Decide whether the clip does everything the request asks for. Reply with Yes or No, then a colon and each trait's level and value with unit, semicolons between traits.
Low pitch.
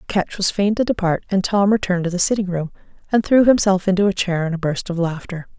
No: high, 190 Hz